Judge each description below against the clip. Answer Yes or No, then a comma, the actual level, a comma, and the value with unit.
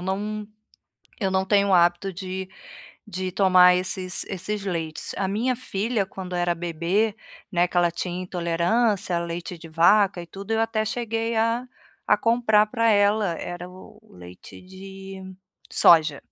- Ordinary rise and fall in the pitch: Yes, average, 3.2 semitones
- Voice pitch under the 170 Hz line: No, high, 190 Hz